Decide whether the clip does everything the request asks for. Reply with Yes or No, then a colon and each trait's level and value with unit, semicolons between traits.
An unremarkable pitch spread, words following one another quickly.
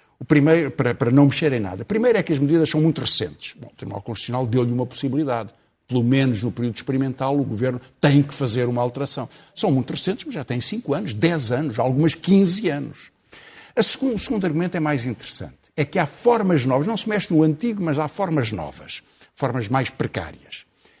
Yes: average, 4.9 semitones; fast, 210 wpm